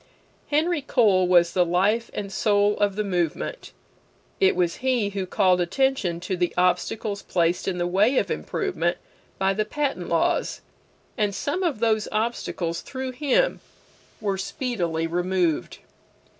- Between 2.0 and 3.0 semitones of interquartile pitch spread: No, wide, 5.4 semitones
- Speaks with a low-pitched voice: No, high, 200 Hz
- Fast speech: No, average, 145 wpm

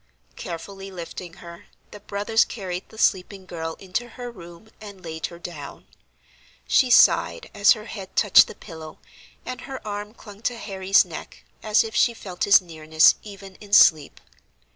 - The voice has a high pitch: Yes, high, 195 Hz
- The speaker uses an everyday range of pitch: Yes, average, 3.7 semitones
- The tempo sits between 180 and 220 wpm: No, average, 165 wpm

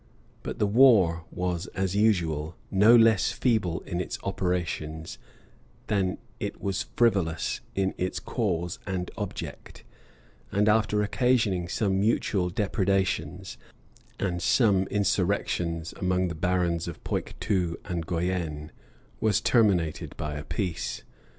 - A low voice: Yes, very low, 95 Hz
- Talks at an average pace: No, slow, 120 wpm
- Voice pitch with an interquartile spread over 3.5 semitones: No, average, 3.1 semitones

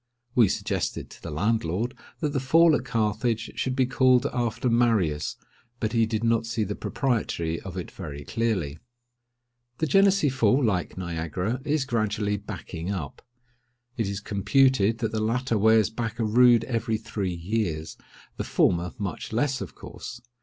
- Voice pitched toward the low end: Yes, low, 110 Hz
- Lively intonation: No, average, 4.2 semitones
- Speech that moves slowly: No, average, 155 wpm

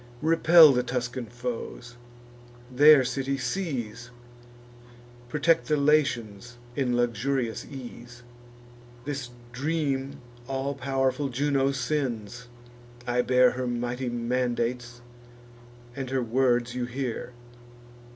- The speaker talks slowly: Yes, slow, 95 wpm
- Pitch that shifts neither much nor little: No, narrow, 2.2 semitones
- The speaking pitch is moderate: No, low, 125 Hz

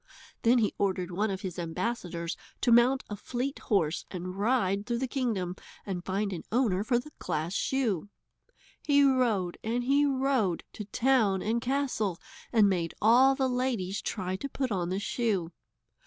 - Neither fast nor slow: Yes, average, 170 wpm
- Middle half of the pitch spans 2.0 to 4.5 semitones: No, average, 5.3 semitones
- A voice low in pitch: No, high, 215 Hz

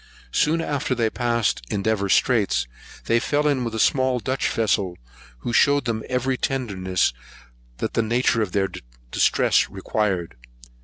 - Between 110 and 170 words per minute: Yes, average, 150 wpm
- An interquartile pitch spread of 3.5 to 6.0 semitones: Yes, average, 4.4 semitones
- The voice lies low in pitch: Yes, low, 115 Hz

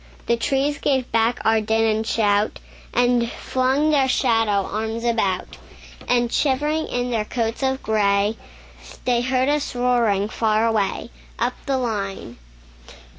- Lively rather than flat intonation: No, average, 2.9 semitones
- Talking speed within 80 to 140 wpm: Yes, slow, 135 wpm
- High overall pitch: Yes, high, 235 Hz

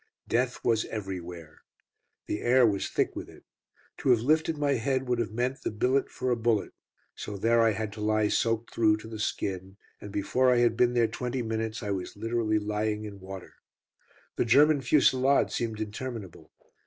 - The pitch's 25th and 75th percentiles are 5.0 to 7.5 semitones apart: No, average, 2.8 semitones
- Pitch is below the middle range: Yes, low, 115 Hz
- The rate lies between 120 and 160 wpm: No, average, 185 wpm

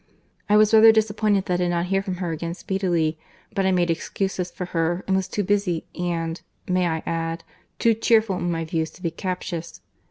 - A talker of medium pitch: Yes, medium, 180 Hz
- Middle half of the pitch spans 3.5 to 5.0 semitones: No, average, 2.7 semitones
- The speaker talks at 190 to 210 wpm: Yes, average, 195 wpm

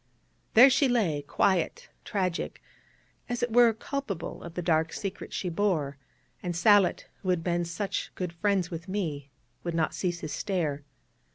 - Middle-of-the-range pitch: Yes, medium, 180 Hz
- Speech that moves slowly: No, average, 160 wpm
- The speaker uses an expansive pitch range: No, average, 3.7 semitones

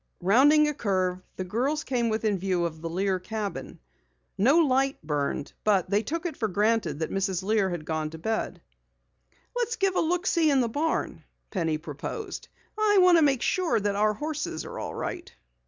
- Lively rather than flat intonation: Yes, wide, 8.5 semitones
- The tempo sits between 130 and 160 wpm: No, average, 185 wpm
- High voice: Yes, high, 215 Hz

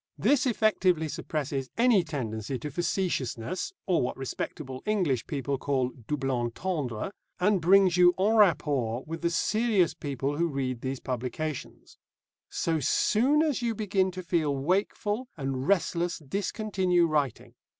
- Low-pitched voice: No, medium, 165 Hz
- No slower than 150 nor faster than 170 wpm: No, slow, 135 wpm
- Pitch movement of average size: No, wide, 6.2 semitones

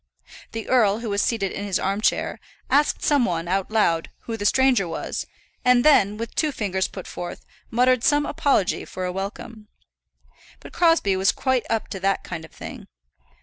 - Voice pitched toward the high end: Yes, high, 210 Hz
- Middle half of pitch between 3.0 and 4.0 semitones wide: No, average, 4.6 semitones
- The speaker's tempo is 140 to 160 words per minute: No, average, 185 wpm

